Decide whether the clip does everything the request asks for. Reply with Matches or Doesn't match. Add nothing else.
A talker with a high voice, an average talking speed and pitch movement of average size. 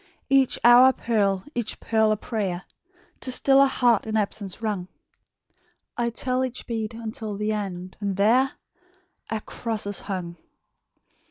Matches